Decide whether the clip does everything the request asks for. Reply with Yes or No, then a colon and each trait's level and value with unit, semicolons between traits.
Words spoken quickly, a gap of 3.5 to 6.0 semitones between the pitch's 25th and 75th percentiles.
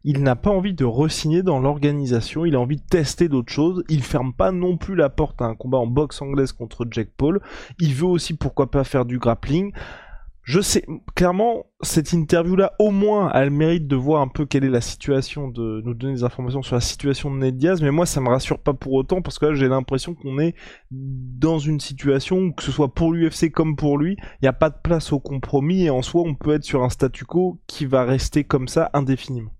Yes: fast, 245 wpm; average, 3.8 semitones